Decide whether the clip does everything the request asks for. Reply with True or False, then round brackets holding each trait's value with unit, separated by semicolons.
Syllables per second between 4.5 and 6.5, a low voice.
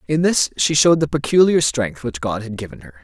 True (5.7 syllables/s; 125 Hz)